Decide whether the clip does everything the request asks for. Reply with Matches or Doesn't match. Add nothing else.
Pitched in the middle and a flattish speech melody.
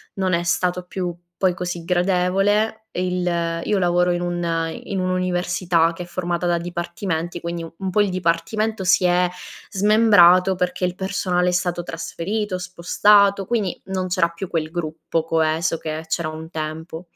Matches